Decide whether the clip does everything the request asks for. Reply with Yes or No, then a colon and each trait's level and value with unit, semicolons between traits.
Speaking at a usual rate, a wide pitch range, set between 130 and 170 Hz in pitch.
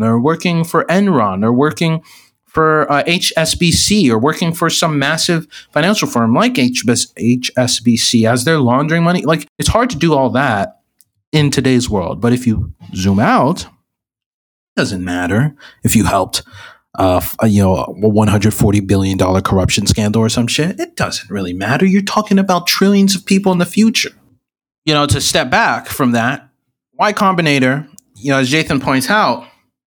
Yes: average, 175 wpm; wide, 7.0 semitones; medium, 140 Hz